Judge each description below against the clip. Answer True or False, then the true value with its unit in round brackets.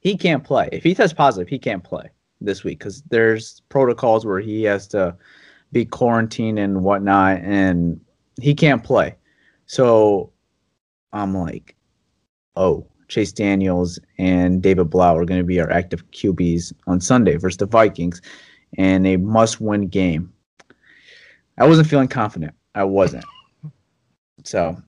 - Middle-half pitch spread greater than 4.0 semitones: True (4.4 semitones)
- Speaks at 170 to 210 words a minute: False (140 wpm)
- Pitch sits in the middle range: False (100 Hz)